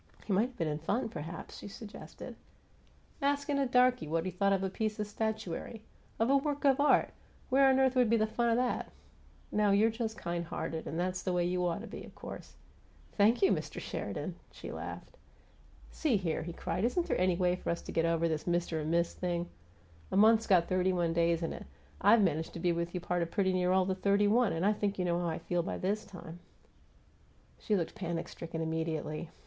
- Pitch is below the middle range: No, medium, 185 Hz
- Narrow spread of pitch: No, average, 4.6 semitones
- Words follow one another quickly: Yes, fast, 230 wpm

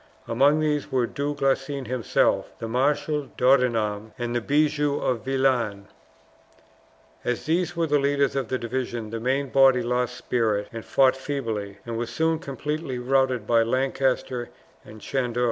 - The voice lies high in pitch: No, low, 130 Hz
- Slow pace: No, average, 150 wpm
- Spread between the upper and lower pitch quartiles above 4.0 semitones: No, average, 3.1 semitones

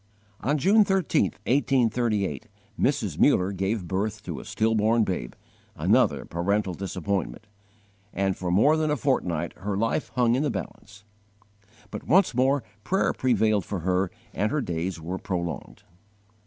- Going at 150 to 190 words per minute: No, average, 140 wpm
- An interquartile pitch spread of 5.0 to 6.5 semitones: Yes, wide, 5.5 semitones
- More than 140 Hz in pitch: No, low, 105 Hz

